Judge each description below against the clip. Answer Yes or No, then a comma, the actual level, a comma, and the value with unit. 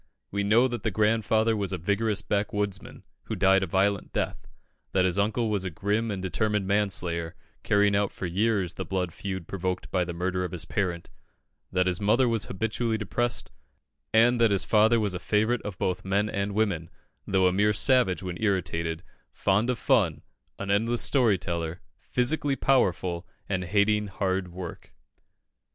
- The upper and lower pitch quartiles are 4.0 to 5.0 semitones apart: No, average, 2.9 semitones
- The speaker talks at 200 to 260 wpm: No, average, 170 wpm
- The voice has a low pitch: Yes, low, 100 Hz